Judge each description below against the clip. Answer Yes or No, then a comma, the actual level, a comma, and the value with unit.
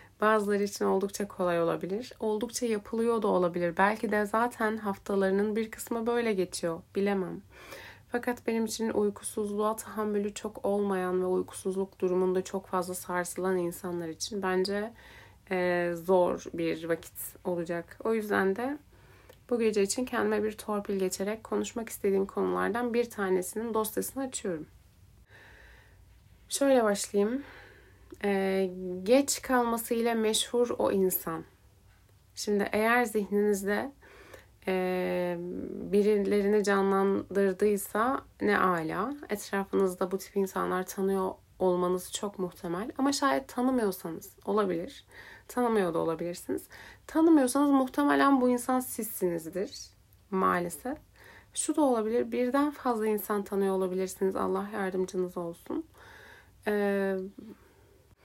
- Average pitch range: Yes, average, 3.5 semitones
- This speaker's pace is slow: No, average, 110 wpm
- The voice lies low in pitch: No, high, 200 Hz